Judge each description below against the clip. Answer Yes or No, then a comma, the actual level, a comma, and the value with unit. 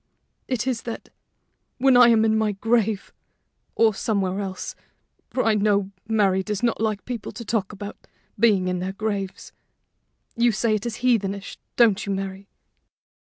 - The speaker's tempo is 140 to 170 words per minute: Yes, average, 160 wpm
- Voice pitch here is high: Yes, high, 215 Hz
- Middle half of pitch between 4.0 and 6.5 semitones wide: No, average, 2.7 semitones